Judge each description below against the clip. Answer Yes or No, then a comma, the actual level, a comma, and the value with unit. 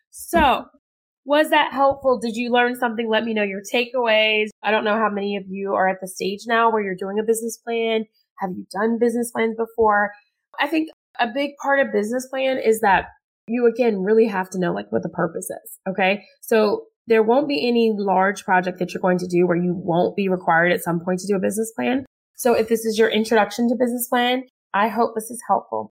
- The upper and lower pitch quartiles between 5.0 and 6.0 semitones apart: No, average, 3.8 semitones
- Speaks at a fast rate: Yes, fast, 225 wpm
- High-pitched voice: Yes, high, 225 Hz